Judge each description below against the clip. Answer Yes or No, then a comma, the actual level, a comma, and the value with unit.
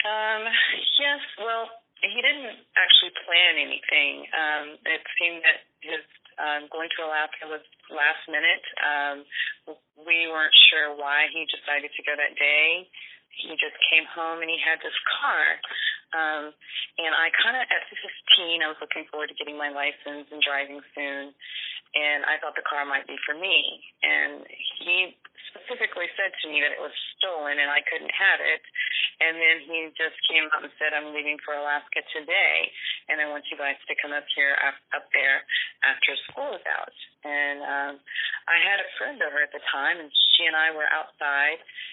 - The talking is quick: No, average, 180 wpm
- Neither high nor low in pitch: Yes, medium, 155 Hz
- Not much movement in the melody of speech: Yes, narrow, 2.0 semitones